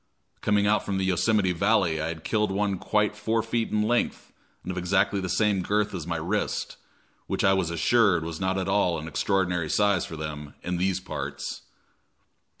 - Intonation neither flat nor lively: Yes, average, 3.4 semitones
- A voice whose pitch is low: Yes, very low, 95 Hz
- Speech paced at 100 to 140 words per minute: No, average, 190 wpm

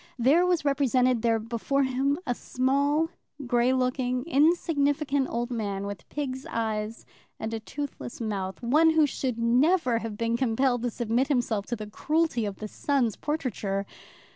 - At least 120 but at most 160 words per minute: Yes, average, 155 wpm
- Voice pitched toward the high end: Yes, very high, 250 Hz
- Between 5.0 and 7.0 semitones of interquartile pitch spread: No, average, 3.8 semitones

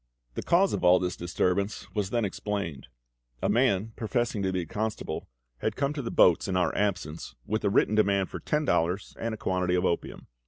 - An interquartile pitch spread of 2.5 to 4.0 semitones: Yes, average, 3.5 semitones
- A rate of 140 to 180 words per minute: No, fast, 205 wpm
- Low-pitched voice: Yes, low, 100 Hz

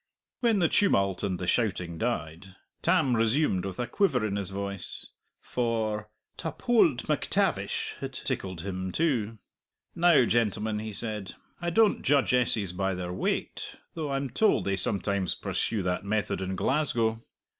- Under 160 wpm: Yes, average, 150 wpm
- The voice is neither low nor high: No, low, 110 Hz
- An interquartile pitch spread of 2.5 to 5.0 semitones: No, wide, 5.4 semitones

